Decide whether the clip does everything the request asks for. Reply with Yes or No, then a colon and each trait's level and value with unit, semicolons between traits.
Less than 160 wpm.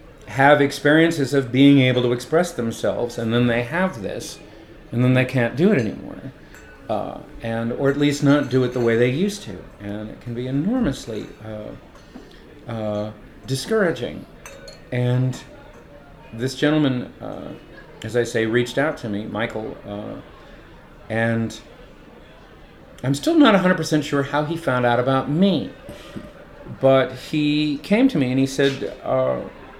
Yes: average, 150 wpm